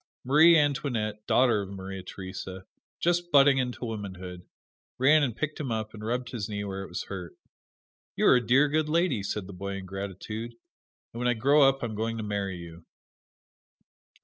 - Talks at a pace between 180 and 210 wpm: Yes, average, 190 wpm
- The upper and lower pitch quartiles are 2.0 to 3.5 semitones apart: No, wide, 5.6 semitones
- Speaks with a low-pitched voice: Yes, low, 110 Hz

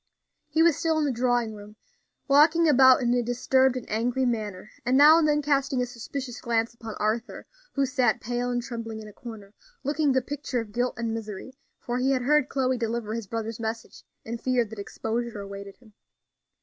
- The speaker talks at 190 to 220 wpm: Yes, average, 200 wpm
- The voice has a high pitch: Yes, high, 245 Hz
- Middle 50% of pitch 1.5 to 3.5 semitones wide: Yes, average, 2.9 semitones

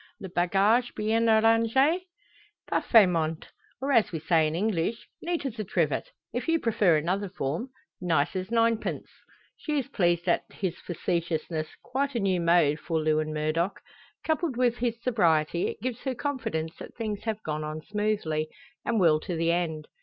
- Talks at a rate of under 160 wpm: No, average, 165 wpm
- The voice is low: No, high, 195 Hz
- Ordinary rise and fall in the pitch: No, wide, 6.1 semitones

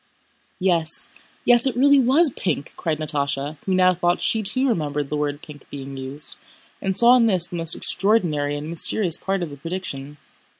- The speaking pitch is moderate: Yes, medium, 170 Hz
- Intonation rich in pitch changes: Yes, wide, 5.8 semitones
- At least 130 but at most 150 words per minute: No, average, 180 wpm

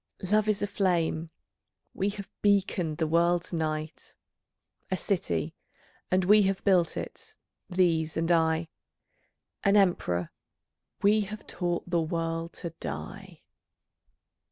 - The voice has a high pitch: No, medium, 175 Hz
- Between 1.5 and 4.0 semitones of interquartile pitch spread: Yes, average, 3.4 semitones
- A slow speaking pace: Yes, slow, 120 wpm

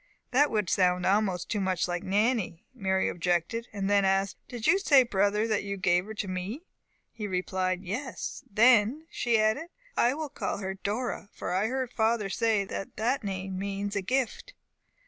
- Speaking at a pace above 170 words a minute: Yes, average, 180 wpm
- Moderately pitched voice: No, high, 205 Hz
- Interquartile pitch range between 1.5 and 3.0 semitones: No, average, 3.6 semitones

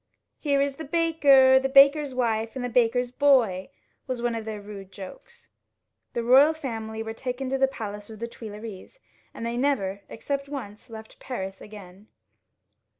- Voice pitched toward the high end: Yes, high, 240 Hz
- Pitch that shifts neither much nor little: Yes, average, 4.0 semitones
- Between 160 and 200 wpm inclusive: Yes, average, 165 wpm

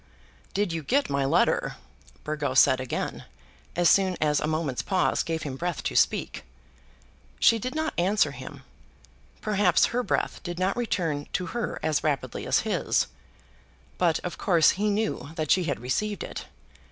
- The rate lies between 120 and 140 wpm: No, average, 165 wpm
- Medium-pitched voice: Yes, medium, 175 Hz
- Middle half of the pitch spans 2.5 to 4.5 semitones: No, average, 5.2 semitones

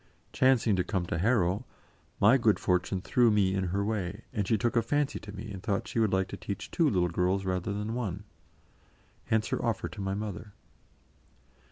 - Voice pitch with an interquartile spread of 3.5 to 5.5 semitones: No, average, 2.9 semitones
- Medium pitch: No, low, 100 Hz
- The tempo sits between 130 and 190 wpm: No, average, 200 wpm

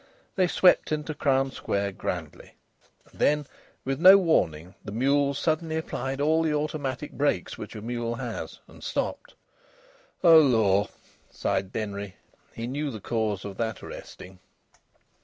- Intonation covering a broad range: Yes, wide, 6.1 semitones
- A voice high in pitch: No, low, 135 Hz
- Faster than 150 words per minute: No, average, 140 wpm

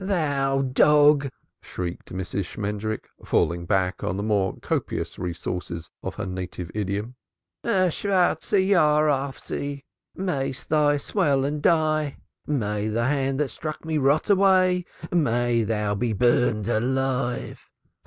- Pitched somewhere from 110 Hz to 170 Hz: Yes, low, 135 Hz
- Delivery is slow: Yes, slow, 130 wpm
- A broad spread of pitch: Yes, wide, 6.3 semitones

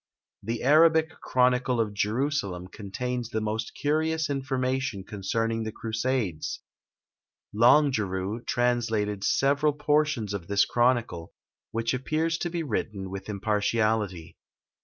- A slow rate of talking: Yes, slow, 110 wpm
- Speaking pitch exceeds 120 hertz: No, low, 115 Hz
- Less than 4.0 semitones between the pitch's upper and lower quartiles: No, average, 4.8 semitones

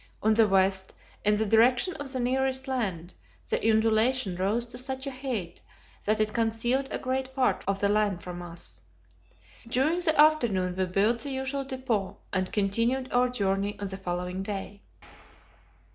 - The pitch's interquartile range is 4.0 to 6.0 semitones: Yes, average, 5.0 semitones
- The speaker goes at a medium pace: Yes, average, 165 wpm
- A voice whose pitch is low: No, high, 225 Hz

